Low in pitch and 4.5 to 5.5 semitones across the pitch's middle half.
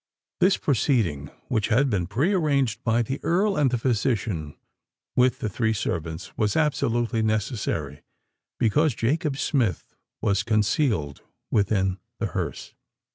Yes: low, 115 Hz; average, 5.0 semitones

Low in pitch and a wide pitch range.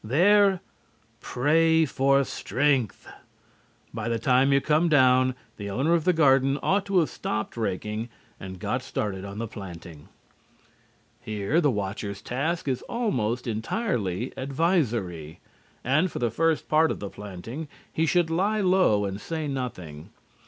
Yes: low, 130 Hz; wide, 7.3 semitones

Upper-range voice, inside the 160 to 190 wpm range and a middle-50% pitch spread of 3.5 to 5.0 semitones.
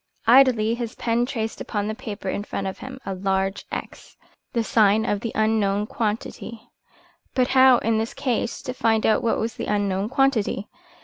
No: high, 220 Hz; average, 180 wpm; narrow, 2.6 semitones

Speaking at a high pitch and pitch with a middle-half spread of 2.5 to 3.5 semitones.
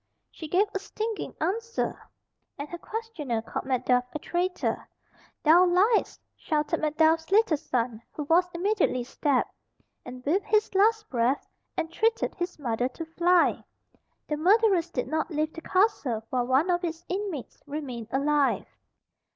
No: very high, 325 Hz; wide, 5.5 semitones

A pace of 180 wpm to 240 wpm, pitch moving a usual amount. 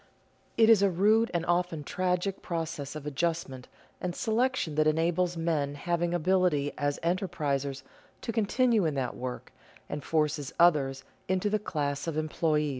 No: average, 150 wpm; average, 3.9 semitones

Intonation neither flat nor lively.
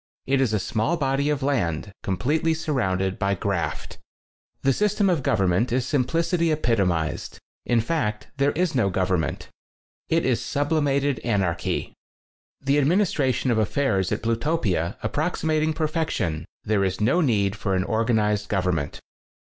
No: wide, 7.3 semitones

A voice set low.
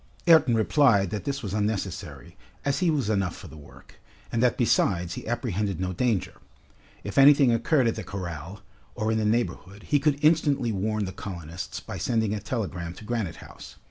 Yes: low, 110 Hz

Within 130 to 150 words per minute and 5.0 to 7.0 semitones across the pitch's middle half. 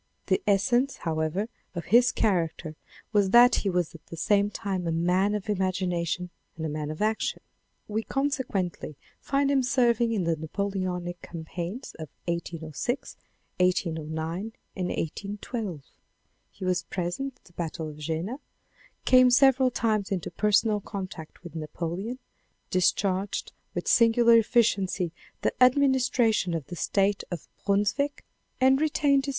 Yes: average, 145 wpm; wide, 5.5 semitones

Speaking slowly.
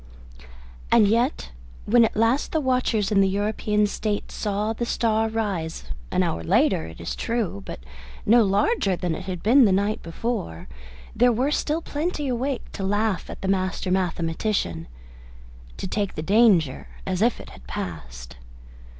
No: average, 160 wpm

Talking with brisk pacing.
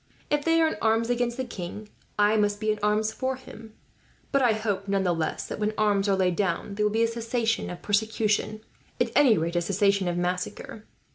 Yes: fast, 220 wpm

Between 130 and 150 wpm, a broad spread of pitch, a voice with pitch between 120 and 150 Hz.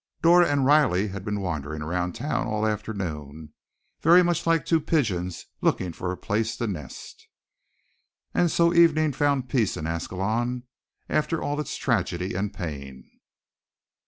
No: average, 145 wpm; wide, 8.6 semitones; low, 110 Hz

